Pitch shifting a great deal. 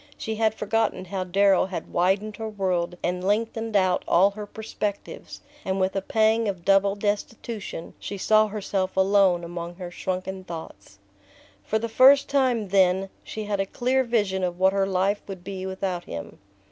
No: narrow, 2.6 semitones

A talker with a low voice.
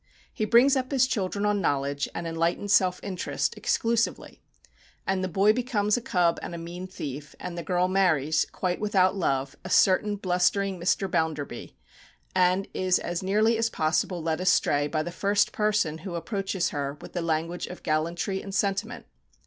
No: medium, 185 Hz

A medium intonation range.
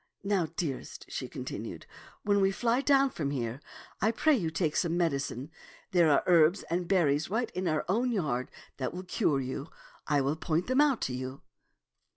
No: wide, 6.1 semitones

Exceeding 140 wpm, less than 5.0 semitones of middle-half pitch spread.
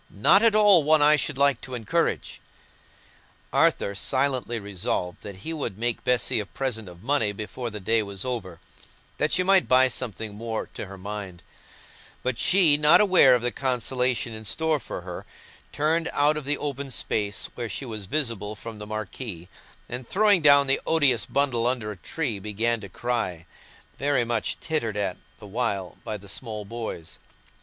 No: average, 175 wpm; wide, 5.4 semitones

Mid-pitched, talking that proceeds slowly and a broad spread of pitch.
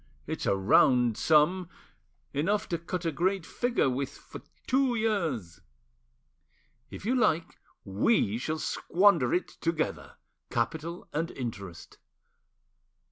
Yes: medium, 165 Hz; slow, 110 wpm; wide, 7.0 semitones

